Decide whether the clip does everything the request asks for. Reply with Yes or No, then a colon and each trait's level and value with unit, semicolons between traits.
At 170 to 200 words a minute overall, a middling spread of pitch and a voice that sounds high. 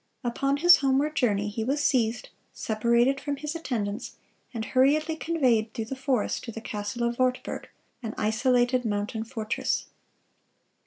No: average, 145 wpm; average, 3.8 semitones; high, 245 Hz